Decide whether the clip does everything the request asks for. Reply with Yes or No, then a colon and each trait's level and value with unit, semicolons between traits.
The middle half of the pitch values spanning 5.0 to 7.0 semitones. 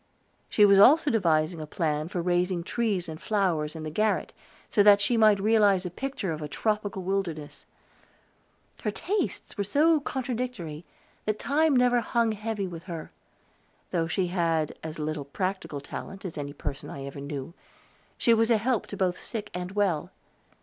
Yes: wide, 5.4 semitones